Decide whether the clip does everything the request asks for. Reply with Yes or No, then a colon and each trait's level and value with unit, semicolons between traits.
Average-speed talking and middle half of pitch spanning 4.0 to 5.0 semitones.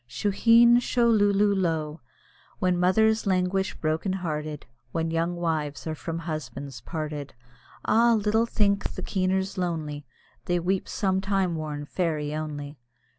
No: slow, 130 wpm; average, 4.3 semitones